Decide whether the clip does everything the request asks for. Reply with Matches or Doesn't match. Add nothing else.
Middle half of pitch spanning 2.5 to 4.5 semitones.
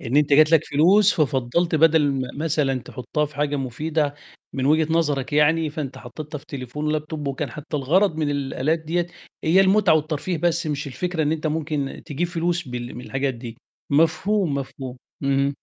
Matches